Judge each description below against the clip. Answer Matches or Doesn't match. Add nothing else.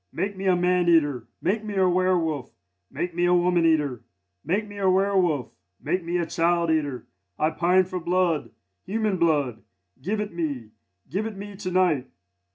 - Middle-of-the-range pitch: Matches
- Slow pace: Doesn't match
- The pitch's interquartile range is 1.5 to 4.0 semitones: Matches